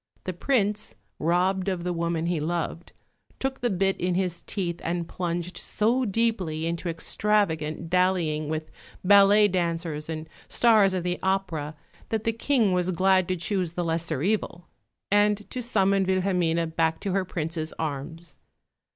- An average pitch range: Yes, average, 3.1 semitones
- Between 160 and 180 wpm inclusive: No, average, 150 wpm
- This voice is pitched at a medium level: Yes, medium, 180 Hz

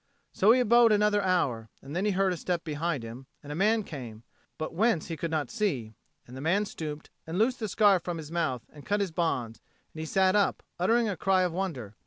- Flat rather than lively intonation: No, wide, 5.5 semitones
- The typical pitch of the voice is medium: Yes, medium, 175 Hz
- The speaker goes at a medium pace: No, fast, 235 wpm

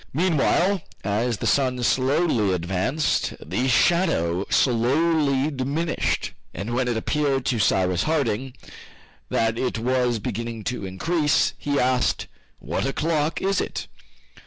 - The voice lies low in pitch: Yes, low, 130 Hz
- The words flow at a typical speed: No, slow, 120 wpm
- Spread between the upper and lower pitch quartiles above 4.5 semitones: Yes, average, 5.0 semitones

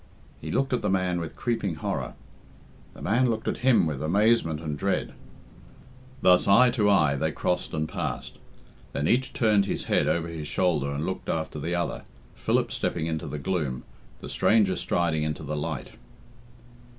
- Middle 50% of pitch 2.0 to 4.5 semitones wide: No, average, 4.9 semitones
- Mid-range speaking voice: No, very low, 85 Hz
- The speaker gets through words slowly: No, average, 175 wpm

